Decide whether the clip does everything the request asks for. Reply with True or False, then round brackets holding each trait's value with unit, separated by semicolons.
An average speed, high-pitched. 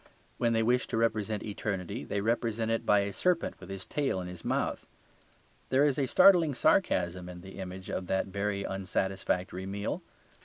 False (180 wpm; 100 Hz)